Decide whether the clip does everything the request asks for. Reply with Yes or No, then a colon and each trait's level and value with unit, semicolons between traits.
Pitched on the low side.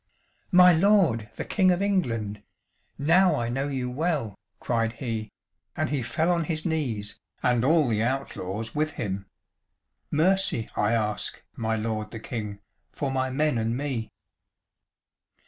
Yes: low, 125 Hz